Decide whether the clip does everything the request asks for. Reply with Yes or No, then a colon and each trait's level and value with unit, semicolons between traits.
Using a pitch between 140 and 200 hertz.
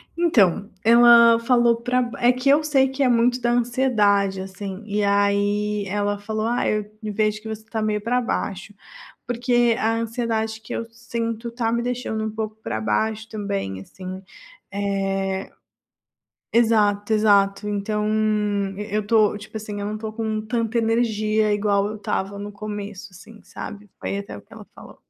No: high, 215 Hz